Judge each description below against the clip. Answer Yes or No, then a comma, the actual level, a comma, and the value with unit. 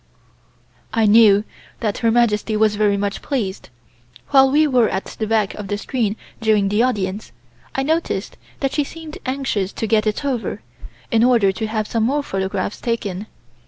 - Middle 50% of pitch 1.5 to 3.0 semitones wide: No, average, 3.7 semitones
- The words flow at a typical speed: Yes, average, 170 wpm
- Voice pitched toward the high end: Yes, high, 220 Hz